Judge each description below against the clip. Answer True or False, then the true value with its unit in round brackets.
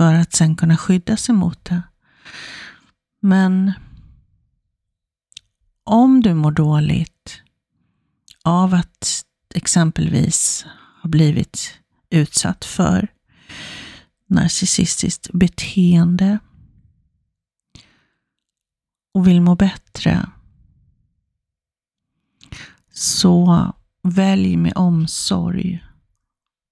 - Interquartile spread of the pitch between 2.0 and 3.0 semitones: True (2.6 semitones)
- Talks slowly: True (65 wpm)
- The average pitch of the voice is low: False (180 Hz)